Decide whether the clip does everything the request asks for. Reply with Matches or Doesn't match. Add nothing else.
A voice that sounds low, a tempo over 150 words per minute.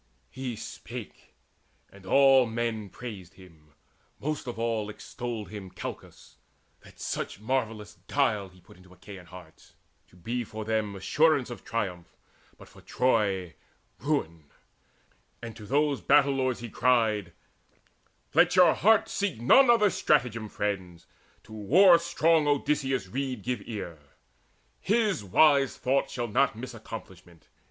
Doesn't match